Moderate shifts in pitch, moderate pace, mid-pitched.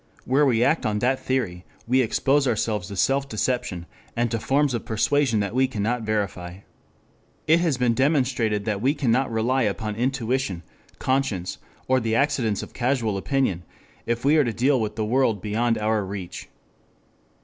No: average, 3.8 semitones; average, 170 wpm; low, 120 Hz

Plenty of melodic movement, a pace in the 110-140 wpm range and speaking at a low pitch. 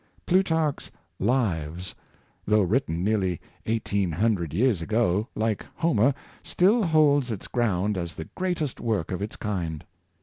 Yes: wide, 6.5 semitones; slow, 135 wpm; low, 105 Hz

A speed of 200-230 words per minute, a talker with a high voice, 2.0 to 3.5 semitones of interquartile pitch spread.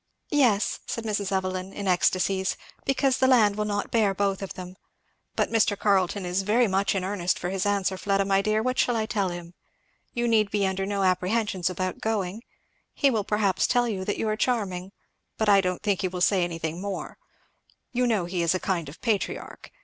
Yes: fast, 205 wpm; high, 195 Hz; average, 2.7 semitones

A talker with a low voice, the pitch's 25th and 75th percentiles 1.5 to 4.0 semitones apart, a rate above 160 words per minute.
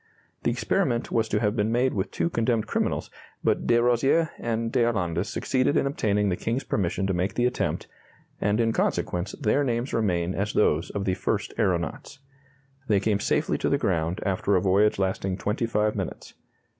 Yes: low, 105 Hz; average, 3.6 semitones; average, 180 wpm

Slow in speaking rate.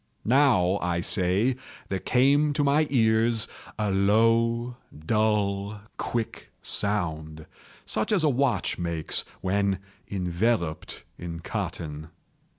Yes: slow, 105 wpm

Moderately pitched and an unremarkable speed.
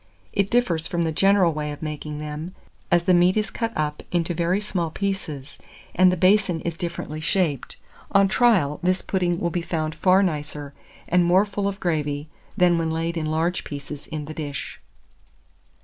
Yes: medium, 170 Hz; average, 180 wpm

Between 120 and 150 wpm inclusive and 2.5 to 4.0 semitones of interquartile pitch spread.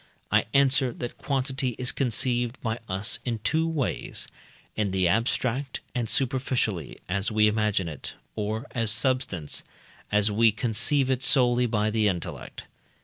Yes: average, 145 wpm; average, 3.5 semitones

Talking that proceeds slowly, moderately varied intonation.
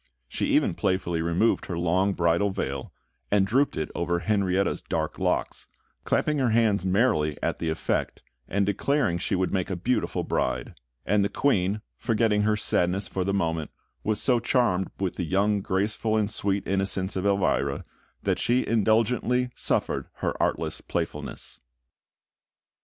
No: average, 150 wpm; average, 3.2 semitones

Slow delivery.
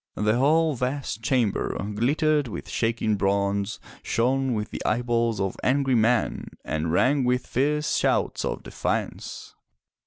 Yes: slow, 130 wpm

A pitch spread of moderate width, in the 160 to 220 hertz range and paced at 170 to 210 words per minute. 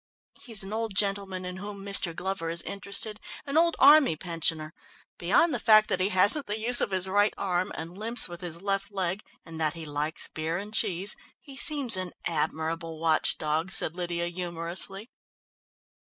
Yes: average, 3.7 semitones; medium, 185 Hz; average, 180 wpm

